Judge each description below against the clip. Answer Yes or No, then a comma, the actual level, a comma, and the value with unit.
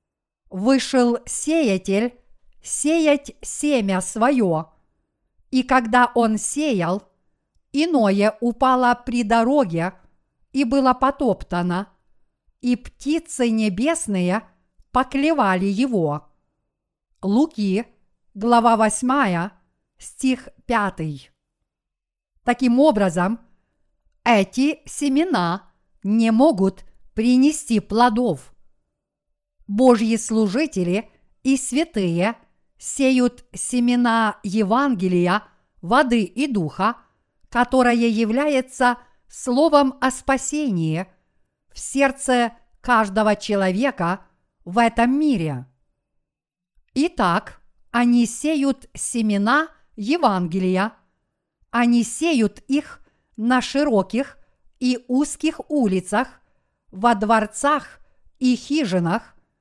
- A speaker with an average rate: No, slow, 75 wpm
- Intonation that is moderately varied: Yes, average, 4.9 semitones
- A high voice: Yes, high, 235 Hz